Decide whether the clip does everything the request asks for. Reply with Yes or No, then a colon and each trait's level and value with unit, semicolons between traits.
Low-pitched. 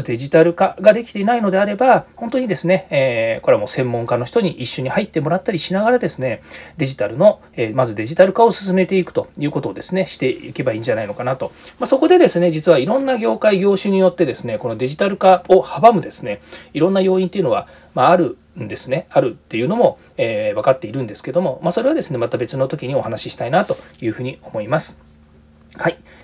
No: medium, 175 Hz